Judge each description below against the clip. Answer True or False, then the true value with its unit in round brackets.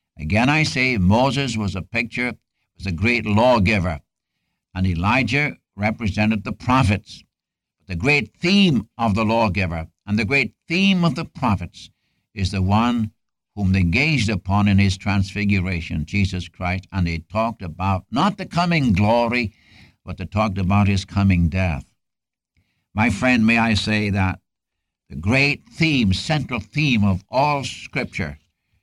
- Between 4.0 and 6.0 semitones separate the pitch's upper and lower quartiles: True (4.3 semitones)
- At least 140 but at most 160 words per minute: True (145 wpm)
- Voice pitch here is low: True (105 Hz)